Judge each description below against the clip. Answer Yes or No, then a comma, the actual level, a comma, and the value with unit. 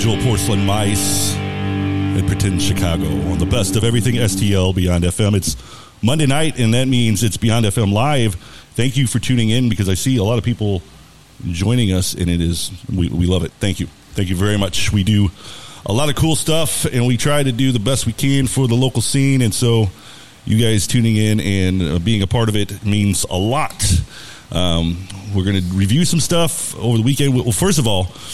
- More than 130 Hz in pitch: No, low, 105 Hz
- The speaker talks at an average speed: No, fast, 210 wpm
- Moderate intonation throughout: Yes, average, 4.0 semitones